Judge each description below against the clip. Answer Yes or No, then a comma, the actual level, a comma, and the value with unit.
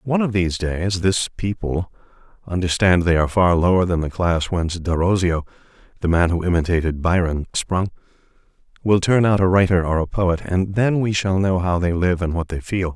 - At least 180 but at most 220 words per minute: Yes, average, 185 wpm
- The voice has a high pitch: No, very low, 90 Hz